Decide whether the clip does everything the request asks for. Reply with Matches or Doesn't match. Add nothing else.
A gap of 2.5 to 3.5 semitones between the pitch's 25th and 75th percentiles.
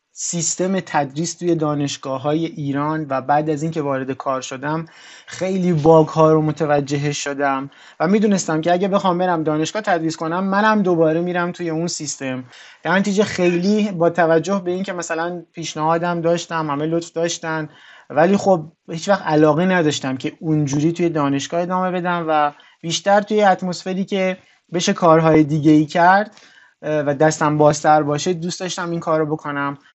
Matches